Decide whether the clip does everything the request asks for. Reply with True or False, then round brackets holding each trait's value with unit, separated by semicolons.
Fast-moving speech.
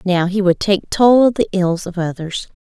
True (225 wpm)